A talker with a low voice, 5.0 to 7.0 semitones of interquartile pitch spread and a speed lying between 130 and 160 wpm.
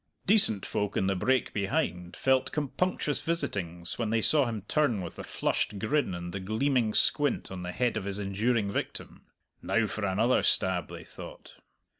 No: low, 105 Hz; wide, 5.4 semitones; average, 175 wpm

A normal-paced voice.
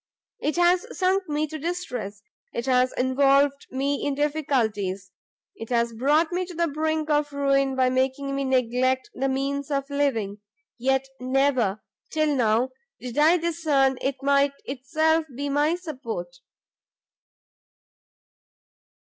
No: slow, 130 wpm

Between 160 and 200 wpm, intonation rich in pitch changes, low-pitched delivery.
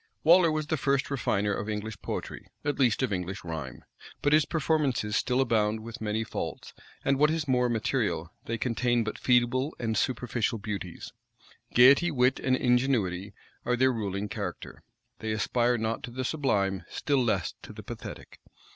No: average, 165 wpm; average, 4.1 semitones; low, 120 Hz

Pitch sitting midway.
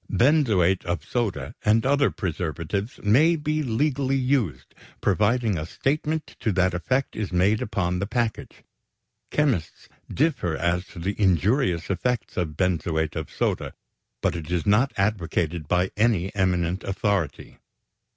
No: low, 100 Hz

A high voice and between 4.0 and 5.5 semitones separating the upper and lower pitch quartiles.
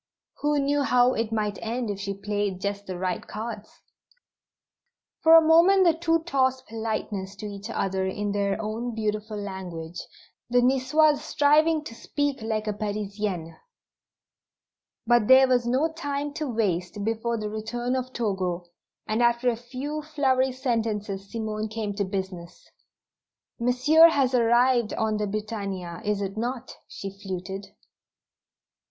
Yes: high, 225 Hz; average, 4.3 semitones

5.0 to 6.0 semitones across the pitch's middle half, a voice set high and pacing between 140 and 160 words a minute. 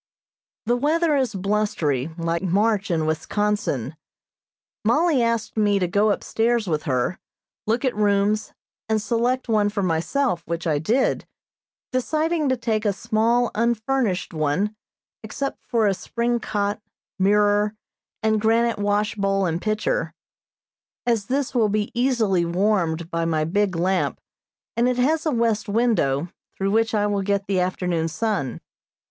No: average, 4.1 semitones; high, 210 Hz; average, 145 wpm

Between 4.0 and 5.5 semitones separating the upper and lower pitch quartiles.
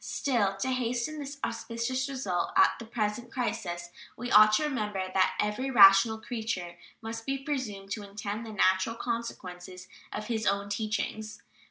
No: average, 3.4 semitones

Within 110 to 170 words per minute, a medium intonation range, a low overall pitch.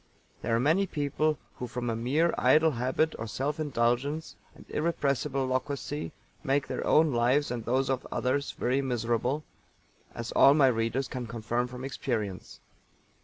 Yes: average, 155 wpm; average, 3.4 semitones; low, 130 Hz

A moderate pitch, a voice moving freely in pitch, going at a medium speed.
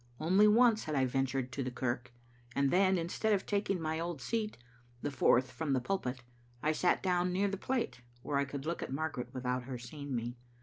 No: medium, 145 Hz; wide, 6.4 semitones; fast, 210 wpm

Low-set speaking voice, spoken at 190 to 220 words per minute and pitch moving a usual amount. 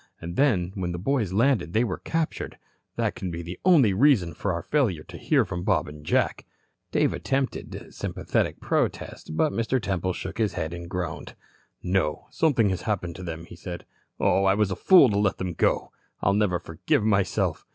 Yes: very low, 95 Hz; average, 195 wpm; average, 4.5 semitones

